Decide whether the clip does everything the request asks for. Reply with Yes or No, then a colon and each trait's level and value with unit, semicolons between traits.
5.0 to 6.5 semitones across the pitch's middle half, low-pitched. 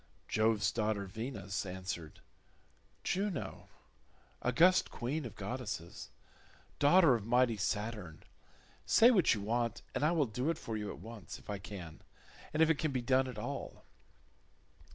Yes: wide, 5.4 semitones; low, 115 Hz